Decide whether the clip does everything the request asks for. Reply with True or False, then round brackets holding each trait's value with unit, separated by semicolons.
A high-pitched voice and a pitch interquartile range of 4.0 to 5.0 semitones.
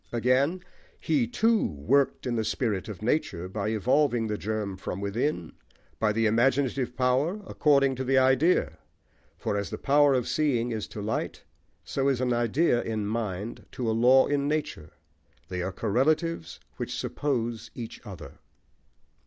False (120 Hz; 4.6 semitones)